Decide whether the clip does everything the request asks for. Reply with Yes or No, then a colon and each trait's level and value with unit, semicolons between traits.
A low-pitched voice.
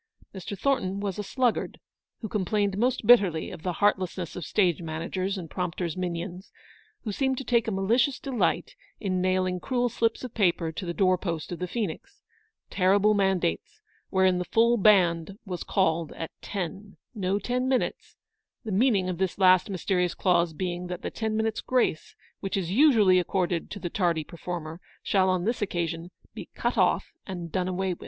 No: high, 190 Hz